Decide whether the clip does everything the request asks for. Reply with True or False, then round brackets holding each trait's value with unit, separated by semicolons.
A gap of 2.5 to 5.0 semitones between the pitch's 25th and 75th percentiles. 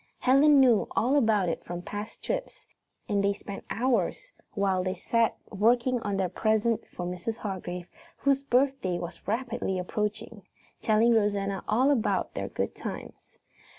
True (4.3 semitones)